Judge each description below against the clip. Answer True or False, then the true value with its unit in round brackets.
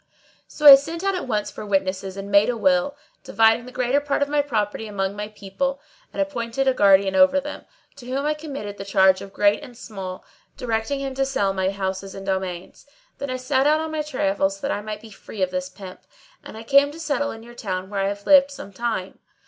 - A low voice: False (225 Hz)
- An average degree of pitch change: False (6.2 semitones)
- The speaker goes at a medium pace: False (230 wpm)